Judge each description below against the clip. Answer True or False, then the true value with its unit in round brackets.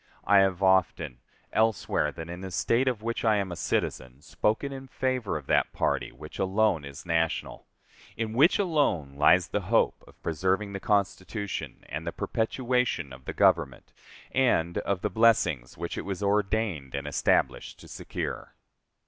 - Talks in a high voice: False (95 Hz)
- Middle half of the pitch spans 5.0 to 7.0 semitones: True (5.4 semitones)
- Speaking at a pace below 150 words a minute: False (165 wpm)